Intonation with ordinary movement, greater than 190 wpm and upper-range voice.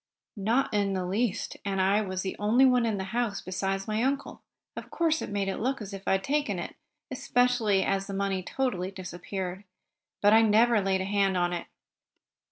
Yes: average, 3.5 semitones; fast, 205 wpm; high, 200 Hz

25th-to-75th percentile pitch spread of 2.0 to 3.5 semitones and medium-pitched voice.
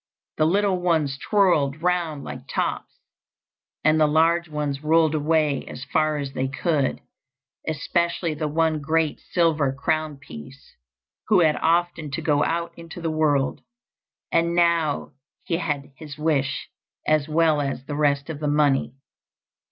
Yes: narrow, 2.4 semitones; medium, 155 Hz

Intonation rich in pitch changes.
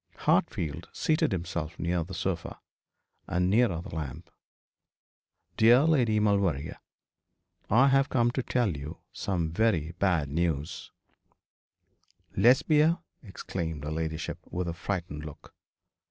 Yes: wide, 5.8 semitones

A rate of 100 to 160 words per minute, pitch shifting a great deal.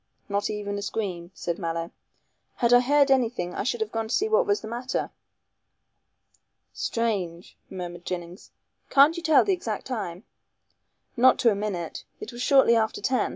No: average, 170 wpm; wide, 6.0 semitones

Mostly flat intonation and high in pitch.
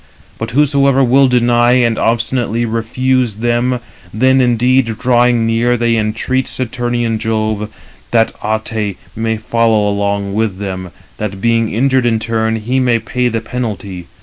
No: narrow, 2.2 semitones; low, 115 Hz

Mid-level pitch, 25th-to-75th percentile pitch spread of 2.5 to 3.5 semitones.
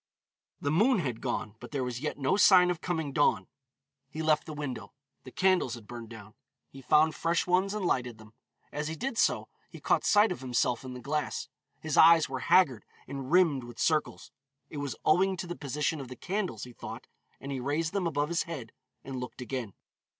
No: medium, 145 Hz; average, 5.3 semitones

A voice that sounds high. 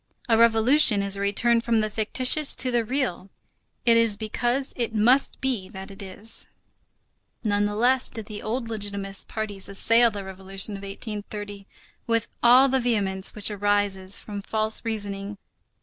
Yes: high, 215 Hz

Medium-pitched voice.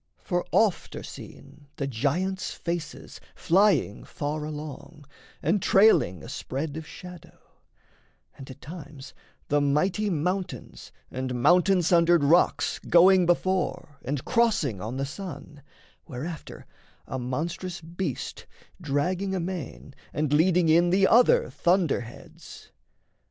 Yes: medium, 165 Hz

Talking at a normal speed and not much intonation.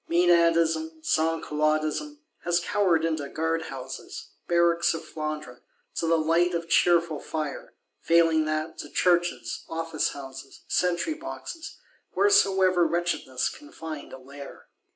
No: slow, 120 wpm; narrow, 2.0 semitones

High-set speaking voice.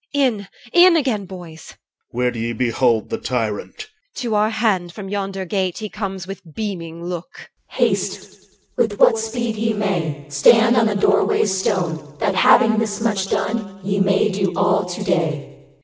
Yes: high, 195 Hz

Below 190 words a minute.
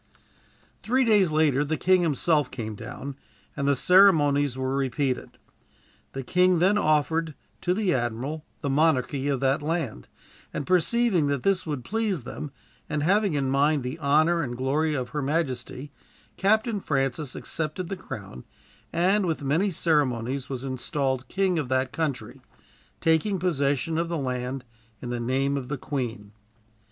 Yes: average, 155 wpm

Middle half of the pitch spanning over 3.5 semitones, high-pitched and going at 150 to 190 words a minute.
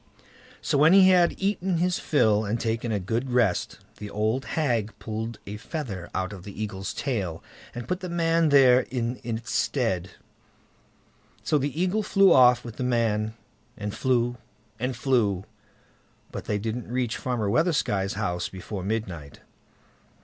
No: average, 4.9 semitones; low, 120 Hz; average, 155 wpm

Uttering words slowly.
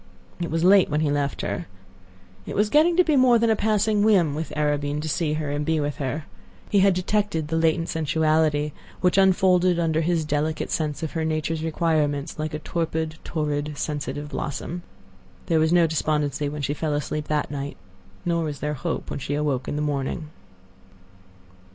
No: average, 190 wpm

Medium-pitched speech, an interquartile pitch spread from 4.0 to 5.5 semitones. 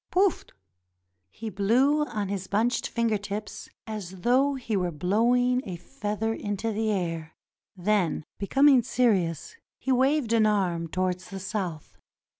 No: high, 210 Hz; average, 4.7 semitones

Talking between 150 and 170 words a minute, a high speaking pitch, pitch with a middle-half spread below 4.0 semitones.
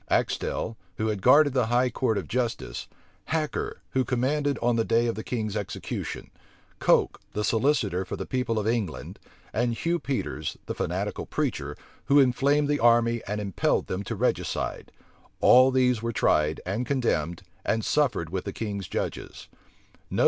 No: average, 160 wpm; low, 115 Hz; average, 3.6 semitones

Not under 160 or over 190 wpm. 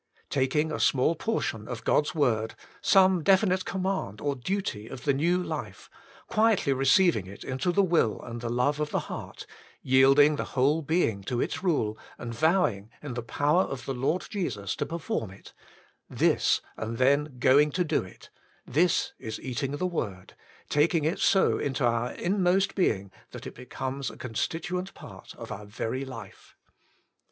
Yes: average, 165 wpm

